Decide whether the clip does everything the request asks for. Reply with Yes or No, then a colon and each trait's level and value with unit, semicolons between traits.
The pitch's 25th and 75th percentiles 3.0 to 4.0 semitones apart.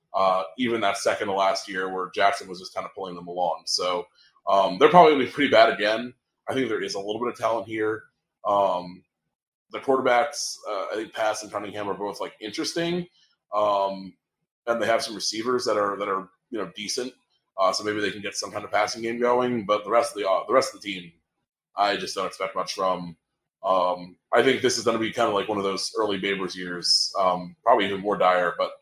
Yes: average, 3.7 semitones